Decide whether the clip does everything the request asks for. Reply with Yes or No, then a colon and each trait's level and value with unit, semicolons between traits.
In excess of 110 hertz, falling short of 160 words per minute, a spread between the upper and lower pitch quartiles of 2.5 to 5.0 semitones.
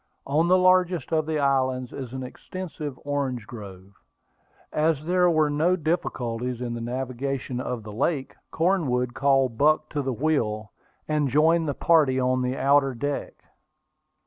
Yes: medium, 140 Hz; average, 150 wpm; average, 3.8 semitones